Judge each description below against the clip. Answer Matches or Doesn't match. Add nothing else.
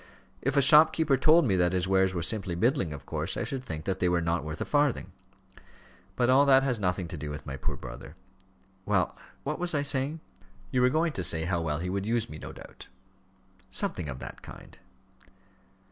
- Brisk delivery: Matches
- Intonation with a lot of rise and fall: Matches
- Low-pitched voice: Matches